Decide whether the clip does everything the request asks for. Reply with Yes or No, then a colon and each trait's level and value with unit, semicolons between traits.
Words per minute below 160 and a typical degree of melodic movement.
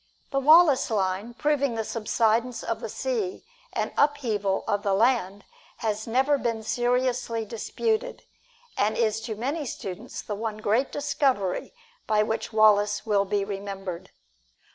Yes: average, 140 wpm; average, 4.2 semitones